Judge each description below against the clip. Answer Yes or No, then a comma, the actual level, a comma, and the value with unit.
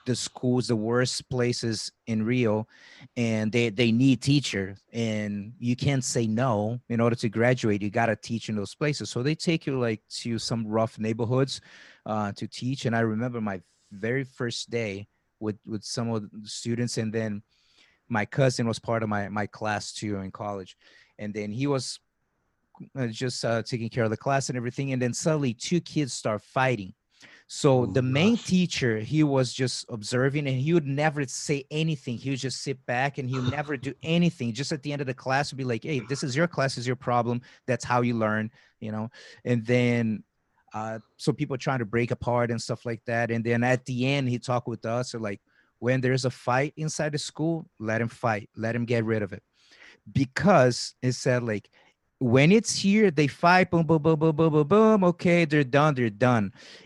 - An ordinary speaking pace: No, fast, 210 wpm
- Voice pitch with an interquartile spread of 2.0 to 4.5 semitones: Yes, average, 3.5 semitones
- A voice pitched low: Yes, low, 125 Hz